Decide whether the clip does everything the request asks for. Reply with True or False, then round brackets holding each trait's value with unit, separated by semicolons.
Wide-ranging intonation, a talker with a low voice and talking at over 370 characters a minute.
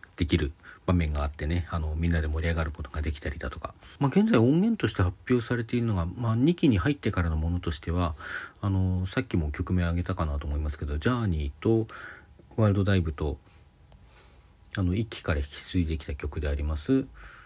True (5.8 semitones; 90 Hz; 410 characters per minute)